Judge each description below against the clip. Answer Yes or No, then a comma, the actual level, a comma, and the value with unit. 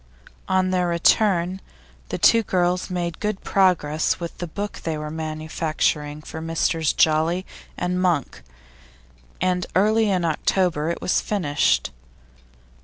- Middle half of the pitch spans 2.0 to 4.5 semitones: Yes, average, 2.9 semitones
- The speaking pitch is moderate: Yes, medium, 175 Hz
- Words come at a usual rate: No, slow, 125 wpm